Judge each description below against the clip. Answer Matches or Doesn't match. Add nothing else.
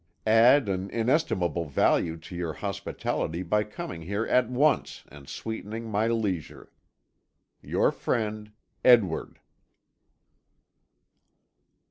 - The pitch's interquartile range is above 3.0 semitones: Matches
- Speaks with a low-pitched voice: Matches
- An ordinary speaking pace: Doesn't match